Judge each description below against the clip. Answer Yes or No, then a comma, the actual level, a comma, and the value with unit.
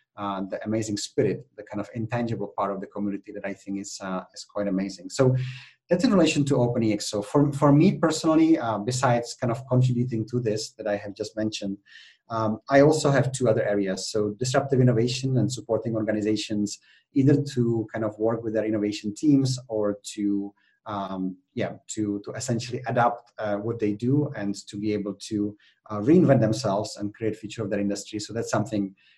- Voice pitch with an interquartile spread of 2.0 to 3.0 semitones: No, average, 3.6 semitones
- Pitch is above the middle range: No, low, 110 Hz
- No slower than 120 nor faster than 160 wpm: No, average, 195 wpm